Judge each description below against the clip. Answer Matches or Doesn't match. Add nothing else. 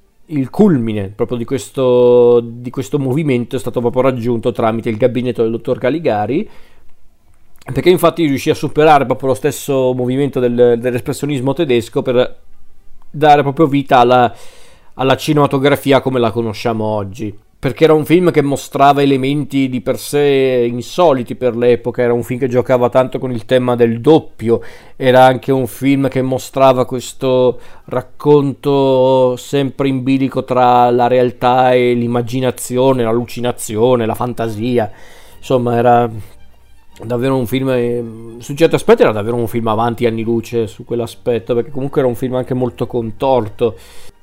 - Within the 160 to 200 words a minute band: Doesn't match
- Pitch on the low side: Matches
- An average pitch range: Doesn't match